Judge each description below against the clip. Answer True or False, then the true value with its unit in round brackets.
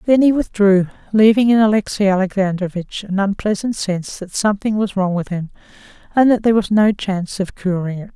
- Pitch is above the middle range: True (200 Hz)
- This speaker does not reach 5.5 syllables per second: False (5.8 syllables/s)